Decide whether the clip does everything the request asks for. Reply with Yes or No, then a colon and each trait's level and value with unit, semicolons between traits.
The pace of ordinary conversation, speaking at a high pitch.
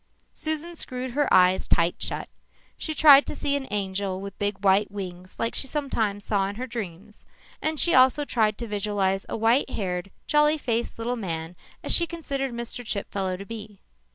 Yes: average, 180 wpm; high, 215 Hz